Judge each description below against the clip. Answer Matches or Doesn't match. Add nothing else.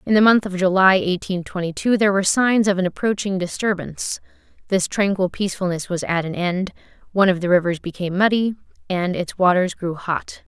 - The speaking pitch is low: Doesn't match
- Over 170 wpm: Matches